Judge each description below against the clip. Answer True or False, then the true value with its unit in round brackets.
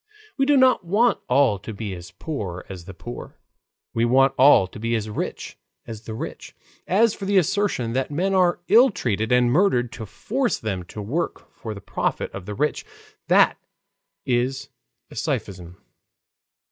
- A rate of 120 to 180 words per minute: True (170 wpm)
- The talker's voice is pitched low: True (125 Hz)